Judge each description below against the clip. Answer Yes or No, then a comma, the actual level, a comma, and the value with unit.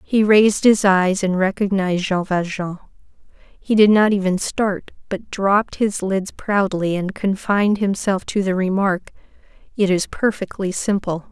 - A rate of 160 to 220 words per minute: No, average, 150 wpm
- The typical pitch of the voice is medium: No, high, 195 Hz